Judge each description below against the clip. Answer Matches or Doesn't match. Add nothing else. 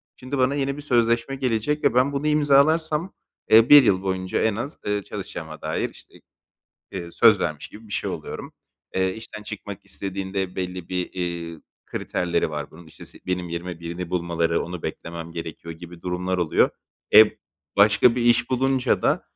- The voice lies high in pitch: Doesn't match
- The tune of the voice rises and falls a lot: Matches